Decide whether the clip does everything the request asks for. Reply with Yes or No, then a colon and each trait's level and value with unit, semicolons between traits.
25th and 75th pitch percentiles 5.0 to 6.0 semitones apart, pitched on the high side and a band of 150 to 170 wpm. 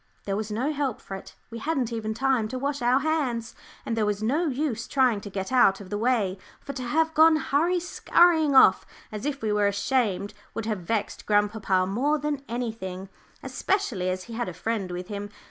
No: wide, 5.4 semitones; high, 230 Hz; fast, 205 wpm